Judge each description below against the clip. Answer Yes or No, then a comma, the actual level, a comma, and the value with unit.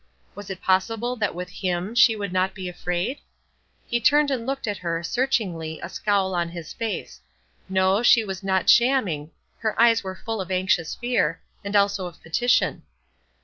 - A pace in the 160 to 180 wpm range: Yes, average, 175 wpm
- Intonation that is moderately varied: Yes, average, 4.1 semitones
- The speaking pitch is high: Yes, high, 195 Hz